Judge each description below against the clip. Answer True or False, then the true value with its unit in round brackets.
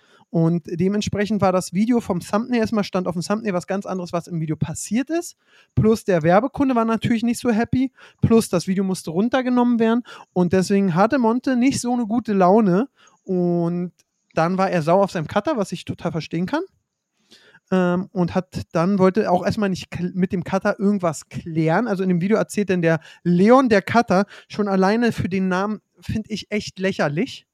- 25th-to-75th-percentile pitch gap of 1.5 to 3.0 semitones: False (3.5 semitones)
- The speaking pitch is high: True (195 Hz)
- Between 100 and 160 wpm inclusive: False (190 wpm)